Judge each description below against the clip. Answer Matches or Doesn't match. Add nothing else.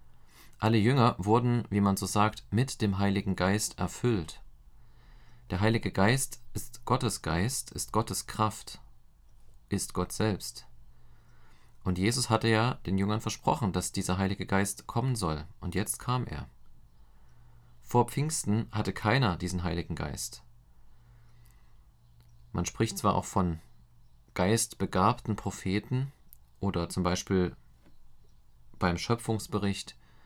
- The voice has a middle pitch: Doesn't match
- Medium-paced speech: Doesn't match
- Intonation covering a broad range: Matches